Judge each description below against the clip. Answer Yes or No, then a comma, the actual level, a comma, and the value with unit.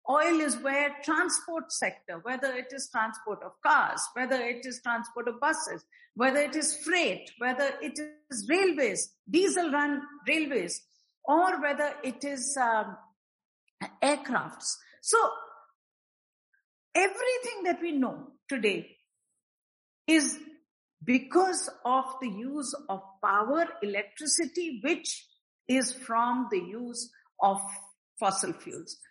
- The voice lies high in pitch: Yes, very high, 280 Hz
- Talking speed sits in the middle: No, slow, 115 wpm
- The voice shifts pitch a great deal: No, average, 4.6 semitones